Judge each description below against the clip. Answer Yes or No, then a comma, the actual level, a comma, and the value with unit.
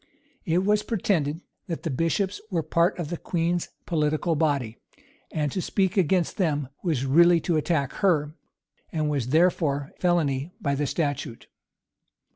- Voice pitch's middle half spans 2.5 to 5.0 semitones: Yes, average, 3.3 semitones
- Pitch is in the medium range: Yes, medium, 160 Hz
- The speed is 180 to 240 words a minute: No, average, 145 wpm